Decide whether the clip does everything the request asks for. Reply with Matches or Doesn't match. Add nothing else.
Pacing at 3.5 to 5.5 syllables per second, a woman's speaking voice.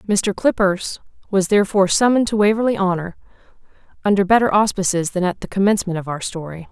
Doesn't match